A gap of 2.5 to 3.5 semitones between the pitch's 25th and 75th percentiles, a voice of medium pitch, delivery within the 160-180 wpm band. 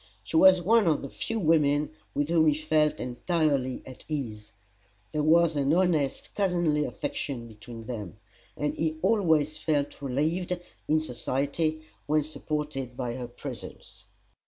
No: average, 3.2 semitones; medium, 150 Hz; average, 140 wpm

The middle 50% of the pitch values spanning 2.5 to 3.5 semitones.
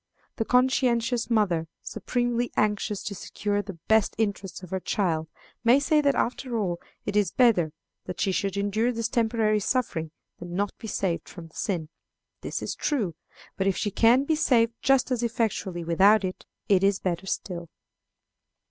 No: average, 4.1 semitones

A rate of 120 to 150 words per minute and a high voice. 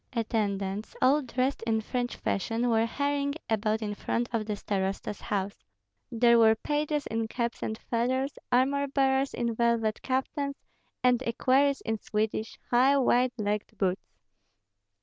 Yes: average, 140 wpm; high, 235 Hz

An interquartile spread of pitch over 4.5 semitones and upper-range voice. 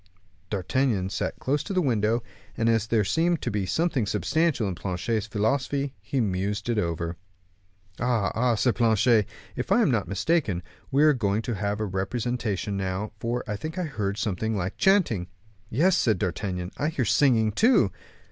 No: average, 4.9 semitones; low, 110 Hz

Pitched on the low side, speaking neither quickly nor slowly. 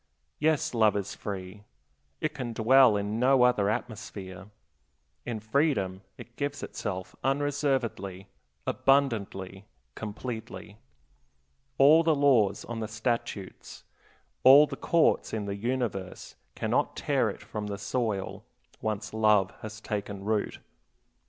No: low, 110 Hz; slow, 120 wpm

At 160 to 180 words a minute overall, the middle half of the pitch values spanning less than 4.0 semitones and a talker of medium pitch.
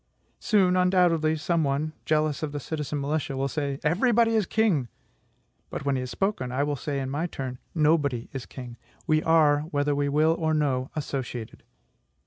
Yes: average, 175 wpm; average, 2.8 semitones; medium, 150 Hz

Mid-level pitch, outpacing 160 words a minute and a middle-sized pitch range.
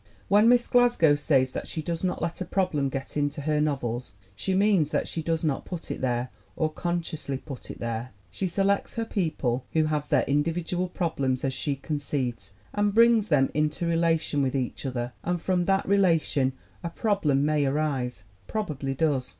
Yes: medium, 155 Hz; average, 185 wpm; average, 4.7 semitones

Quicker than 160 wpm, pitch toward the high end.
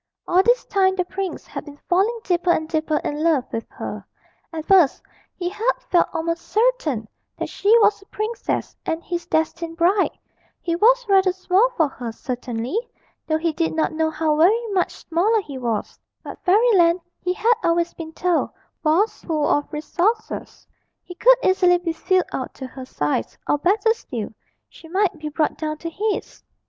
Yes: average, 180 wpm; very high, 345 Hz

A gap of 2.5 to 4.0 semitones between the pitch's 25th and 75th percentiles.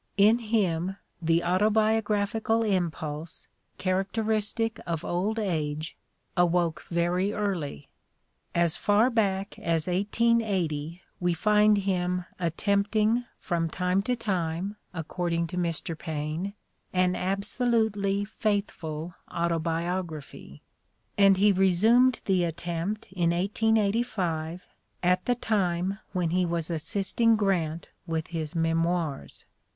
Yes: average, 3.7 semitones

